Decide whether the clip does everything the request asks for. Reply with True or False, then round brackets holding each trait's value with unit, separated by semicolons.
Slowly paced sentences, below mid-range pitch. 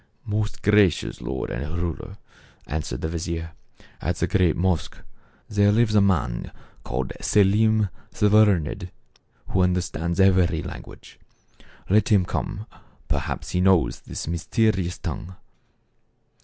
True (130 wpm; 95 Hz)